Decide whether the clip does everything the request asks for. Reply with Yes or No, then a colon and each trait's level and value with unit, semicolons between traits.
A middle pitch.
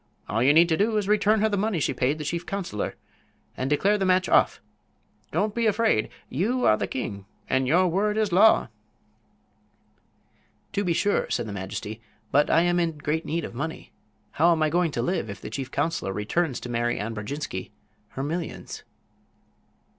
Yes: medium, 165 Hz